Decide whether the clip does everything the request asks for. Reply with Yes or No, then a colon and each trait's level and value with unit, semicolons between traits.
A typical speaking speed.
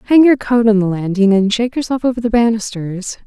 No: fast, 220 wpm